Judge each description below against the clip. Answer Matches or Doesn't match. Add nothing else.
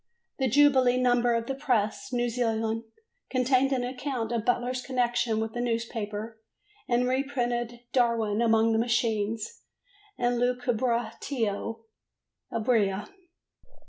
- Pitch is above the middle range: Matches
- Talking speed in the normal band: Doesn't match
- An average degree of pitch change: Doesn't match